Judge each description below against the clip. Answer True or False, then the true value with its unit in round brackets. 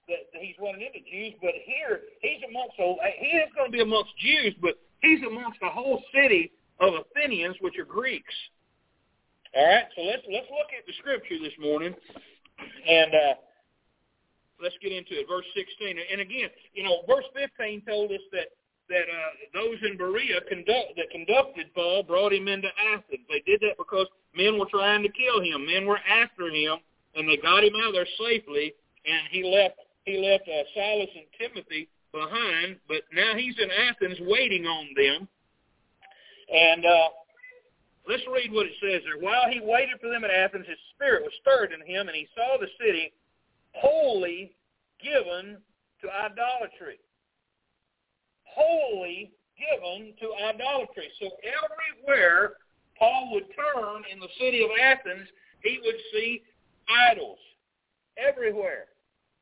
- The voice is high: True (215 Hz)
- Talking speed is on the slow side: False (160 wpm)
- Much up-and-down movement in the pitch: True (8.1 semitones)